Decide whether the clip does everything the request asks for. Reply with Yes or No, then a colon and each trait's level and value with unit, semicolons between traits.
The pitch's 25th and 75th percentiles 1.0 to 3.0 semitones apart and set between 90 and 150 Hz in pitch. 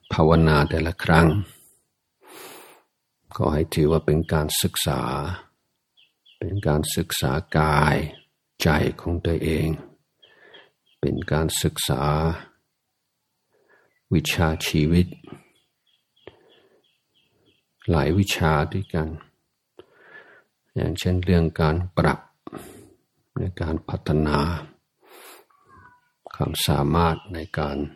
No: average, 2.7 semitones; very low, 80 Hz